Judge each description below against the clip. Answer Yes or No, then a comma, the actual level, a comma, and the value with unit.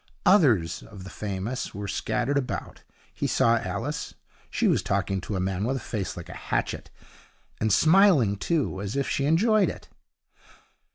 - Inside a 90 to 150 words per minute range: No, average, 165 wpm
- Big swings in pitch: Yes, wide, 6.7 semitones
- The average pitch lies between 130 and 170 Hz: No, low, 110 Hz